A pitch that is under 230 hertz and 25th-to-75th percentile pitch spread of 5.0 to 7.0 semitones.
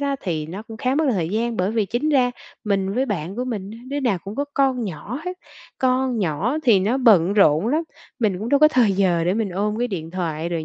Yes: high, 215 Hz; wide, 5.4 semitones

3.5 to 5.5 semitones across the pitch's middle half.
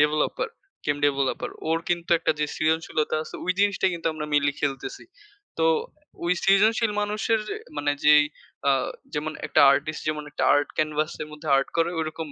No: narrow, 2.6 semitones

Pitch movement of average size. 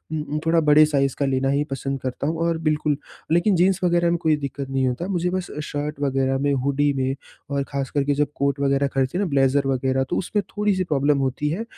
Yes: average, 3.4 semitones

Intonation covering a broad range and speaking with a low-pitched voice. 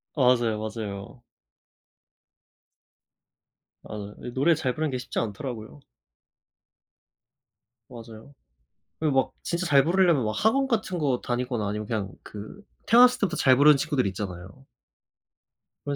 Yes: wide, 6.4 semitones; low, 125 Hz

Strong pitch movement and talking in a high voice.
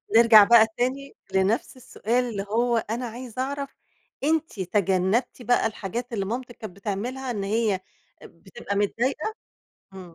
No: average, 3.8 semitones; high, 230 Hz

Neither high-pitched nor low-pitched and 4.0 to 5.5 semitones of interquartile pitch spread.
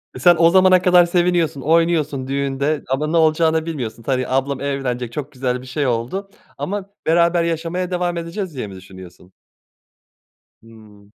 Yes: medium, 150 Hz; average, 5.1 semitones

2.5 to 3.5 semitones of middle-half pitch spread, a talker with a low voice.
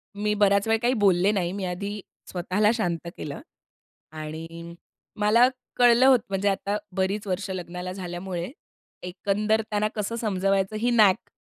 No: average, 2.9 semitones; high, 195 Hz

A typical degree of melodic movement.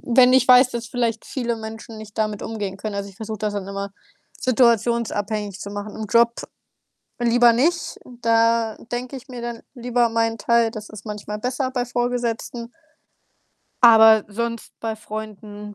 No: narrow, 2.1 semitones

